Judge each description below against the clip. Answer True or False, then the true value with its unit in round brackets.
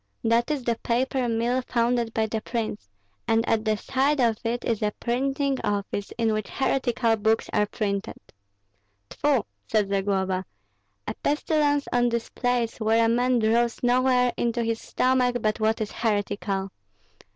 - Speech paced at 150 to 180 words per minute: True (160 wpm)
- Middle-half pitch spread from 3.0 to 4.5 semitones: False (2.4 semitones)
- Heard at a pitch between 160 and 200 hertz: False (230 Hz)